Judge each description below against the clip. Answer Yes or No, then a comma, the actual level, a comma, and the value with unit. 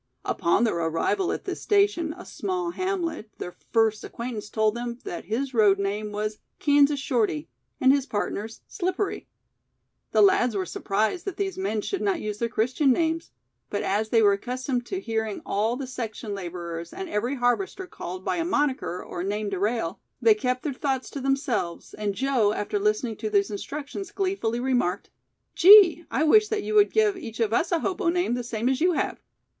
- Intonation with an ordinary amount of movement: No, wide, 8.0 semitones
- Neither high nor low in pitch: No, high, 245 Hz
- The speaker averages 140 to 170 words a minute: No, average, 190 wpm